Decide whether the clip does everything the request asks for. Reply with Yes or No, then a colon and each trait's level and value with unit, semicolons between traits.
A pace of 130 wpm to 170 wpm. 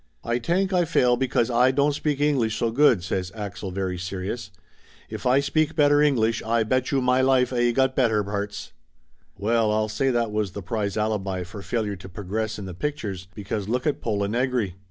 No: average, 190 wpm